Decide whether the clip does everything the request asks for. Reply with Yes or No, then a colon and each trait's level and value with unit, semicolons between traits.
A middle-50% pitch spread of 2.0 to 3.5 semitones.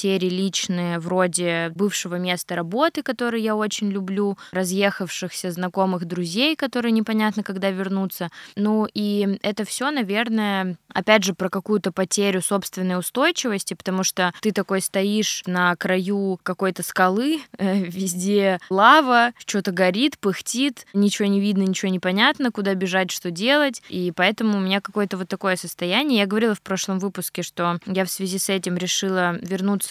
Yes: narrow, 2.4 semitones